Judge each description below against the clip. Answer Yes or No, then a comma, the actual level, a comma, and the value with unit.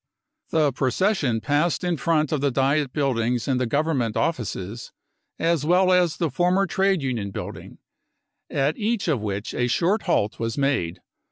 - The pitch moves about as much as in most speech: No, wide, 5.7 semitones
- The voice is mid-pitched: Yes, medium, 145 Hz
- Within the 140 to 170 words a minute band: Yes, average, 160 wpm